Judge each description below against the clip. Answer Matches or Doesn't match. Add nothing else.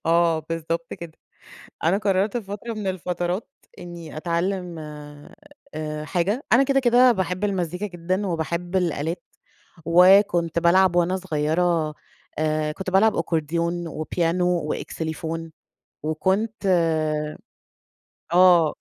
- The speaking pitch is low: Doesn't match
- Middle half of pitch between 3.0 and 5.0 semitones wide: Doesn't match